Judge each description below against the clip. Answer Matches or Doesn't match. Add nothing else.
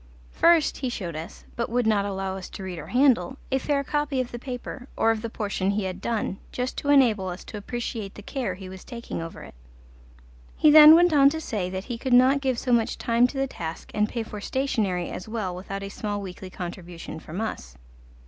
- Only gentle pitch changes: Doesn't match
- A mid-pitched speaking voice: Doesn't match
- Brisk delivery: Matches